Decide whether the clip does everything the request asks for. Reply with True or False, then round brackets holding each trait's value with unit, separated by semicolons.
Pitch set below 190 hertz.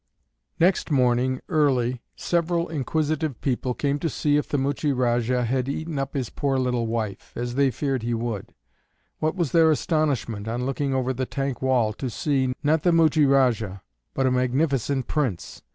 True (135 Hz)